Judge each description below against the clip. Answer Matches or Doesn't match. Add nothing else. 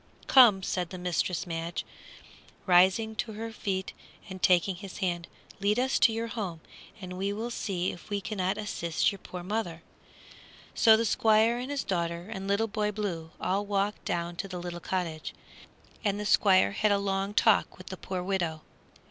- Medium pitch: Doesn't match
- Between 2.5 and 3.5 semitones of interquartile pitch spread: Matches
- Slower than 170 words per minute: Doesn't match